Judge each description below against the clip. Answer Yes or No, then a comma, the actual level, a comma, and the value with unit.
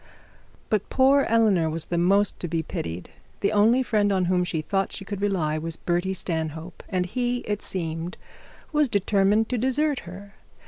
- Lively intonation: No, average, 4.1 semitones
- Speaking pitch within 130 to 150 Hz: No, high, 195 Hz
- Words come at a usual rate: Yes, average, 175 wpm